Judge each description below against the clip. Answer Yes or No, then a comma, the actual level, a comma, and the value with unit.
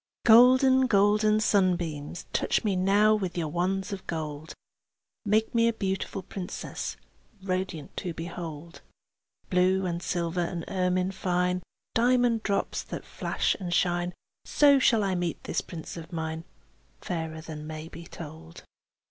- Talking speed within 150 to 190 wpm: No, average, 140 wpm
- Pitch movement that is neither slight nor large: Yes, average, 3.5 semitones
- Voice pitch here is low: No, medium, 180 Hz